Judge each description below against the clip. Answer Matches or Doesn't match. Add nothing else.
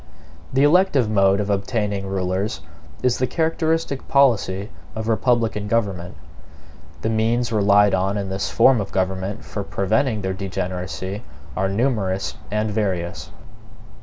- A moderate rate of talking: Doesn't match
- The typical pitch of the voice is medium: Doesn't match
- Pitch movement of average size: Matches